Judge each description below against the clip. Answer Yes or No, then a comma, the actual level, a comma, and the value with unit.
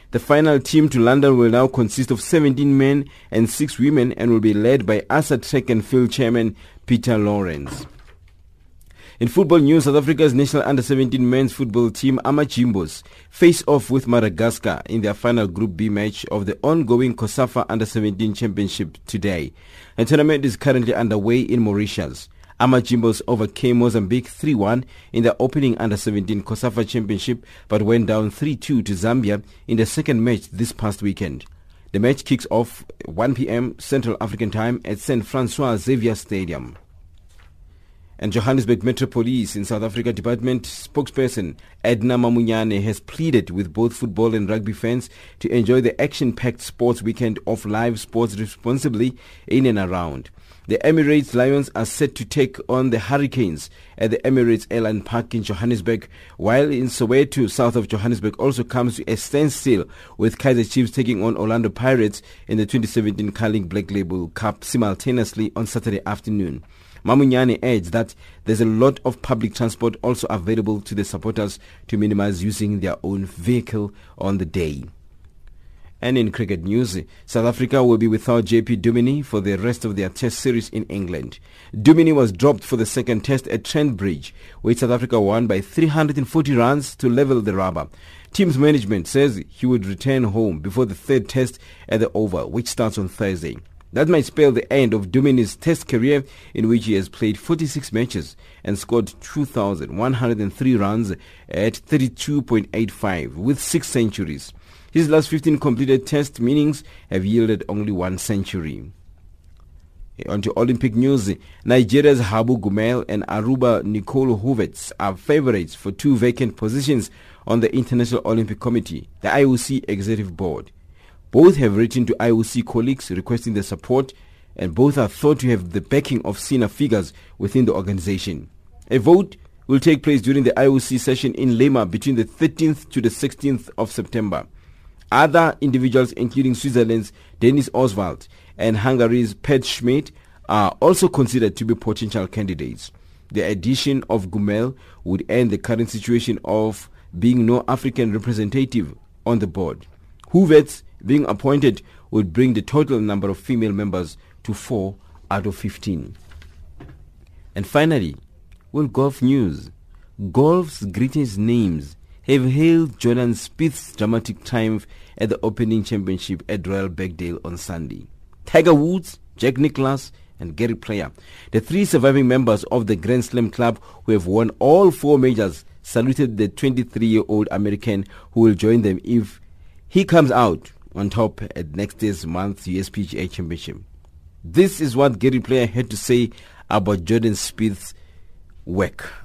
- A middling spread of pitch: Yes, average, 4.7 semitones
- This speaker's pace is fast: No, average, 155 wpm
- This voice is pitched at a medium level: No, low, 115 Hz